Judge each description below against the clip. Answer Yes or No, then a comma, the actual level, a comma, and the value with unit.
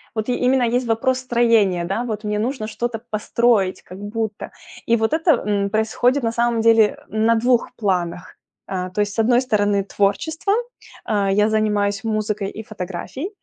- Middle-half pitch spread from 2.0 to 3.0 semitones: Yes, average, 2.7 semitones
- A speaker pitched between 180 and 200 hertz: No, high, 220 Hz